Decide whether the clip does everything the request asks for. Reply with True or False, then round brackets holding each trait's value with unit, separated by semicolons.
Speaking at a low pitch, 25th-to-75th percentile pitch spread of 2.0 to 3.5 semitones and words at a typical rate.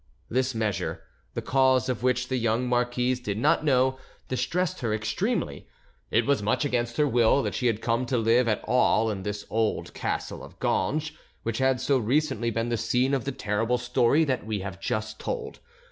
True (125 Hz; 2.9 semitones; 190 wpm)